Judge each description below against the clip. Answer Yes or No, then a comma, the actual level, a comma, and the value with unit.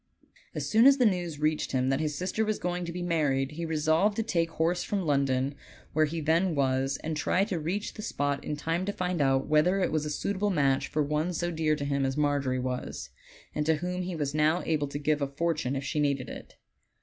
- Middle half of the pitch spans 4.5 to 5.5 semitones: No, average, 3.8 semitones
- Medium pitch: Yes, medium, 155 Hz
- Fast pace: Yes, fast, 235 wpm